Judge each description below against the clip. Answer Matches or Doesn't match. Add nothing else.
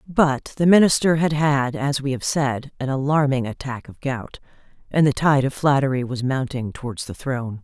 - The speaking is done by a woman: Matches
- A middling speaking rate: Matches